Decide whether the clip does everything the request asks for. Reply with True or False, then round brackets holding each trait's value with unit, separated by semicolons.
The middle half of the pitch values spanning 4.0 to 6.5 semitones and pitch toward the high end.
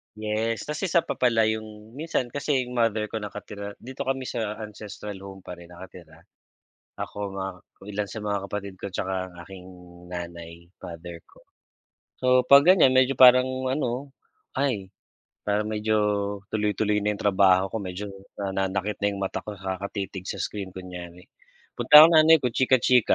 False (4.4 semitones; 105 Hz)